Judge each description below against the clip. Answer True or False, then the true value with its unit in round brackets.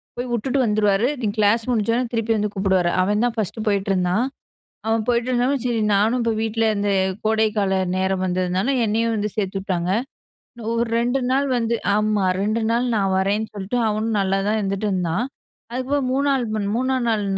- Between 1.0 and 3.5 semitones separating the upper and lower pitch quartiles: True (3.2 semitones)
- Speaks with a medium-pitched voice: False (215 Hz)